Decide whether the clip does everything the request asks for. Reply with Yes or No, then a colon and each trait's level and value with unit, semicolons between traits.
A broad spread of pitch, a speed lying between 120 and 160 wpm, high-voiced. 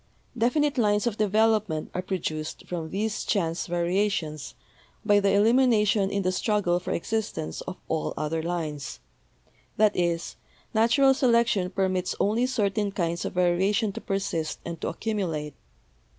No: average, 4.1 semitones; average, 140 wpm; high, 195 Hz